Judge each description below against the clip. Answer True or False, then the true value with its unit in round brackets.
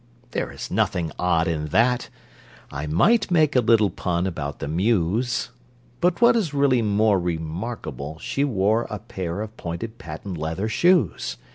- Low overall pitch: True (100 Hz)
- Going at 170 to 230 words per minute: False (155 wpm)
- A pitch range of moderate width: False (6.7 semitones)